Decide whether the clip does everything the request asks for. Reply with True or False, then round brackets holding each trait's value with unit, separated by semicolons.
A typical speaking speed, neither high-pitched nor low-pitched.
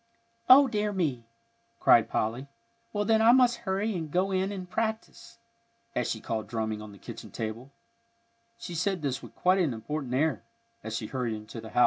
True (185 wpm; 155 Hz)